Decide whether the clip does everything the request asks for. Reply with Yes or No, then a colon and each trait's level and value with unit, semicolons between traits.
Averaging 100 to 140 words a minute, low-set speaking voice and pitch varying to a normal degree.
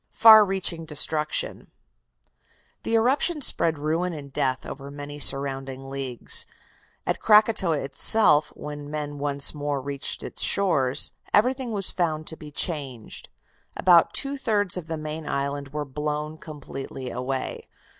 No: slow, 135 wpm; medium, 150 Hz; average, 4.4 semitones